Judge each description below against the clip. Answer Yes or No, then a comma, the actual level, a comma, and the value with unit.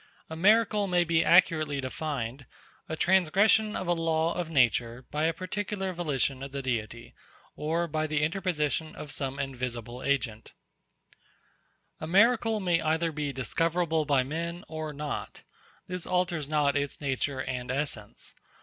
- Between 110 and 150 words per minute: Yes, average, 145 wpm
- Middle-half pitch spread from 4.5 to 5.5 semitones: No, average, 4.1 semitones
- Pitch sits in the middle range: Yes, medium, 155 Hz